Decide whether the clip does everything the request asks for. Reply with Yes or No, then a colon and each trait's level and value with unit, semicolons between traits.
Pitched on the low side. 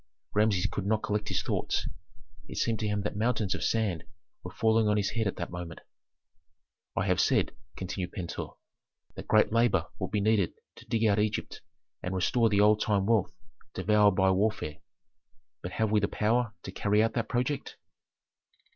Yes: low, 105 Hz